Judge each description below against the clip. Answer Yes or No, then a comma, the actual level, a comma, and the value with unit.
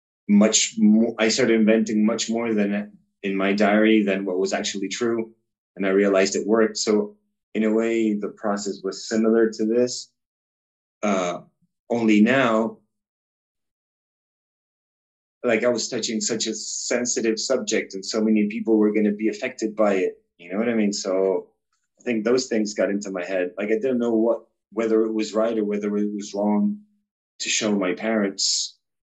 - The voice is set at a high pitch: No, low, 110 Hz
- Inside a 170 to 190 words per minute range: Yes, average, 175 wpm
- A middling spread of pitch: No, narrow, 1.8 semitones